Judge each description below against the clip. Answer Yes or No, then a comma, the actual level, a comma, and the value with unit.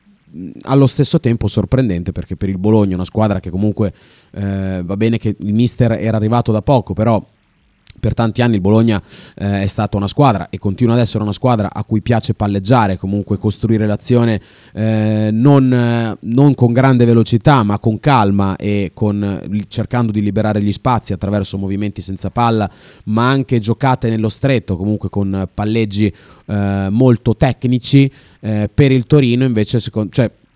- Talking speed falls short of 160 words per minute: No, average, 165 wpm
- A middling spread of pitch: Yes, average, 3.1 semitones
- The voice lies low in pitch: Yes, low, 110 Hz